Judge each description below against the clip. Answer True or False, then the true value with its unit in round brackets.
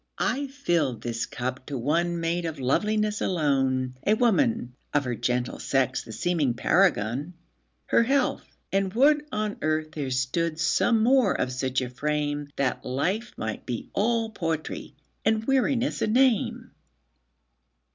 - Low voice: False (160 Hz)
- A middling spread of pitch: False (8.8 semitones)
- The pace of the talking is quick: False (135 wpm)